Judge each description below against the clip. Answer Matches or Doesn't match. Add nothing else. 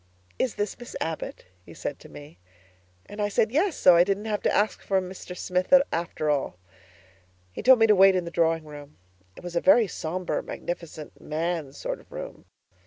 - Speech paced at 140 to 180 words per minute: Doesn't match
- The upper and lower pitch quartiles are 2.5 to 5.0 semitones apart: Matches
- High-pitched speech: Doesn't match